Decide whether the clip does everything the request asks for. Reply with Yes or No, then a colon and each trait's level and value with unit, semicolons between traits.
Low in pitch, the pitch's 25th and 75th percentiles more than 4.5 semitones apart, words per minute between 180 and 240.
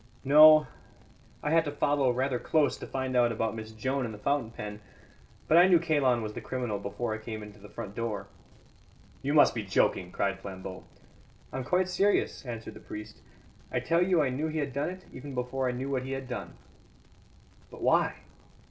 Yes: low, 130 Hz; average, 5.0 semitones; average, 200 wpm